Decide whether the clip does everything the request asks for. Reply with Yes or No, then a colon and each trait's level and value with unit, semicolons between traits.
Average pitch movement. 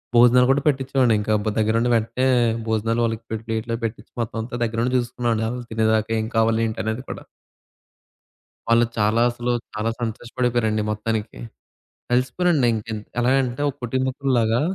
No: narrow, 2.0 semitones